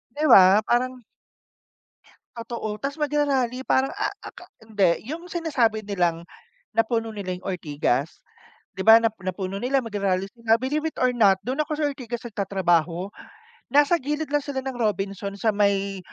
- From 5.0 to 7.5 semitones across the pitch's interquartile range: Yes, wide, 5.5 semitones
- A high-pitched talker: Yes, high, 225 Hz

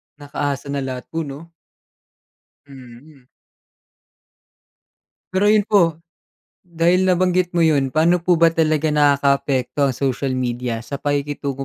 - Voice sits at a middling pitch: Yes, medium, 145 Hz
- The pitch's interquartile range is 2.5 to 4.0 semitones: Yes, average, 3.5 semitones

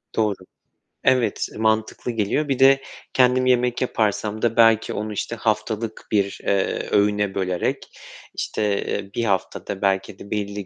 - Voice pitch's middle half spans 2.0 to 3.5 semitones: Yes, narrow, 2.6 semitones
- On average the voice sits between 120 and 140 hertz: No, low, 110 Hz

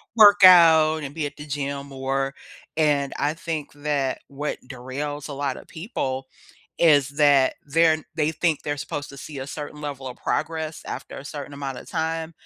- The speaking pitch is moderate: Yes, medium, 145 Hz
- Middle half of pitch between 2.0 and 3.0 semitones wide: Yes, narrow, 2.4 semitones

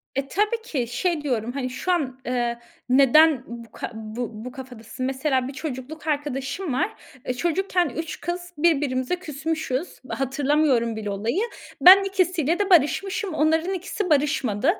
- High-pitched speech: Yes, very high, 285 Hz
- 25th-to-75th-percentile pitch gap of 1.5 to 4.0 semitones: No, average, 5.3 semitones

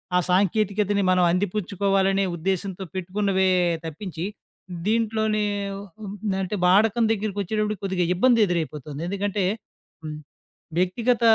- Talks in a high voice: Yes, high, 195 Hz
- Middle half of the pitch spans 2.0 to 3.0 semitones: Yes, narrow, 2.6 semitones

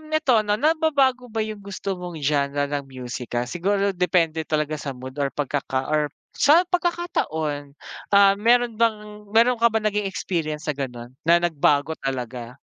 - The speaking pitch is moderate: Yes, medium, 170 Hz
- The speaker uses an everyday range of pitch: No, wide, 7.3 semitones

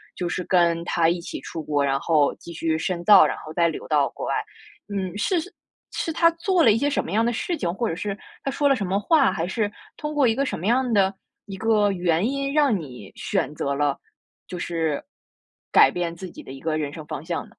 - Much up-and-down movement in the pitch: Yes, wide, 6.0 semitones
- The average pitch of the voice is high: No, medium, 180 Hz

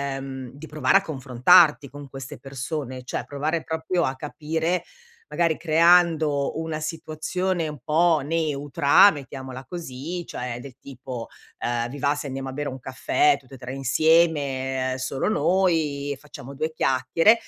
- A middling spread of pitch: Yes, average, 3.5 semitones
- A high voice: No, medium, 145 Hz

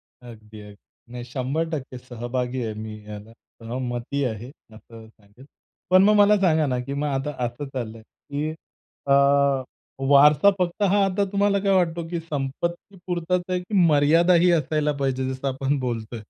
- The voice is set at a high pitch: No, medium, 140 Hz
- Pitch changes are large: Yes, wide, 5.9 semitones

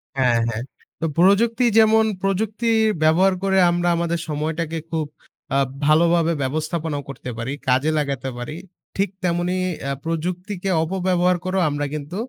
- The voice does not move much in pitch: No, average, 3.9 semitones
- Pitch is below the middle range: No, medium, 170 Hz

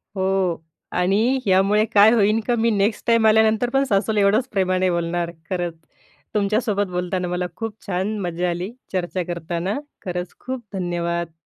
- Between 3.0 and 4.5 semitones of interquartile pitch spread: Yes, average, 3.4 semitones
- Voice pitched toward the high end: Yes, high, 195 Hz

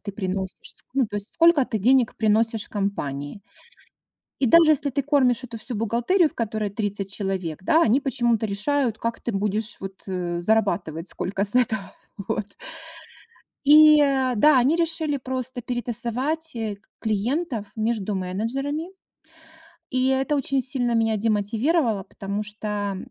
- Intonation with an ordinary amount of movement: Yes, average, 4.8 semitones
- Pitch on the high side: Yes, high, 230 Hz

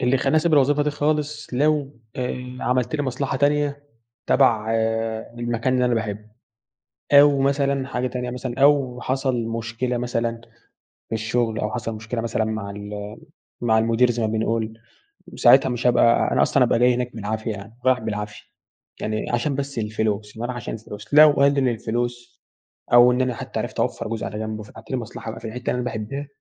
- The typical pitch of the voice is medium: No, low, 120 Hz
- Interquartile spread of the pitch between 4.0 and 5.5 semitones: No, average, 3.2 semitones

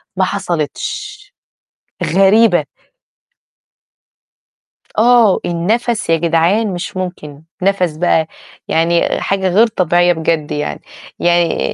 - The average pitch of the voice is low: No, medium, 180 Hz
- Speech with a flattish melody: No, average, 3.6 semitones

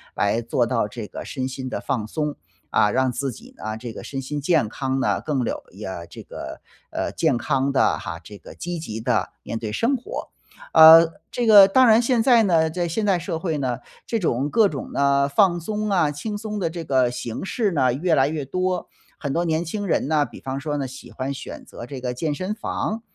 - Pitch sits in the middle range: Yes, medium, 145 Hz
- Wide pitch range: Yes, wide, 6.0 semitones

